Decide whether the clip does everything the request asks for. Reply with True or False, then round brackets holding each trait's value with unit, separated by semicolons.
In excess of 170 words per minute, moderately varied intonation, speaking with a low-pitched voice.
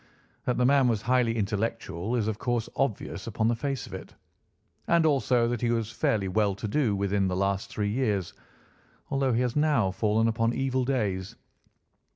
True (185 wpm; 3.5 semitones; 115 Hz)